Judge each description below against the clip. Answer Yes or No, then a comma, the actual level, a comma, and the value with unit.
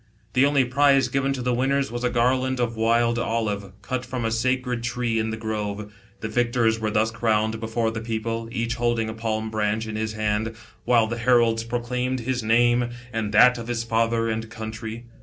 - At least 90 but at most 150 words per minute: No, average, 195 wpm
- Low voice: Yes, low, 115 Hz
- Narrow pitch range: Yes, narrow, 1.8 semitones